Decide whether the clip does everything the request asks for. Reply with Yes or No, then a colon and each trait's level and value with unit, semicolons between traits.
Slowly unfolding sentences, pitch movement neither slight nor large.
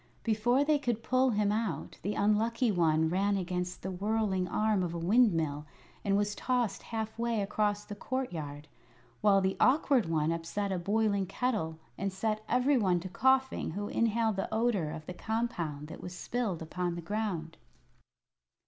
No: average, 165 wpm; average, 4.3 semitones